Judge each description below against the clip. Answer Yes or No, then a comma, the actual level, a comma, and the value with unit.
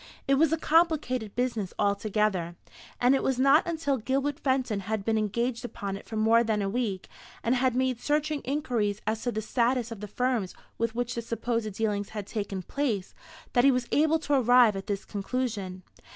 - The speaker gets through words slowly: No, average, 195 wpm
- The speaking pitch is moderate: No, high, 235 Hz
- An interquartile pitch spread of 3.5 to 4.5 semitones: Yes, average, 3.9 semitones